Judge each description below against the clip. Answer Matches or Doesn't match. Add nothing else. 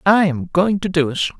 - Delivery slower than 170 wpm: Doesn't match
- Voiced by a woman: Doesn't match